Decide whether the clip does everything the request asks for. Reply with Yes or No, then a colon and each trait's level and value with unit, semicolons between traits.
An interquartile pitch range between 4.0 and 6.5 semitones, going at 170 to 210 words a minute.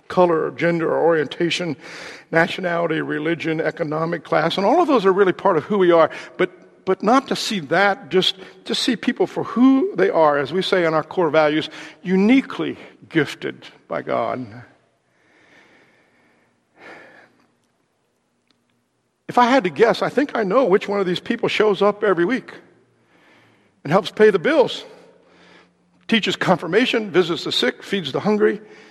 No: average, 4.6 semitones; average, 160 wpm